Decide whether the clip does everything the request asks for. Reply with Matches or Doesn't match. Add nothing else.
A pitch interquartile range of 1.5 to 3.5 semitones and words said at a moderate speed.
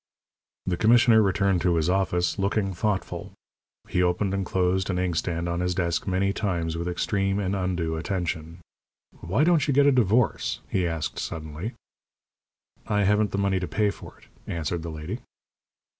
Matches